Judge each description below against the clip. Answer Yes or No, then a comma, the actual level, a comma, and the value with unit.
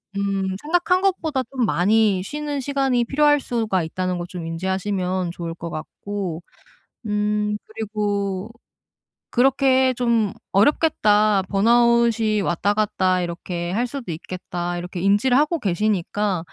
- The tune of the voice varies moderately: Yes, average, 4.7 semitones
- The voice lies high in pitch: Yes, high, 210 Hz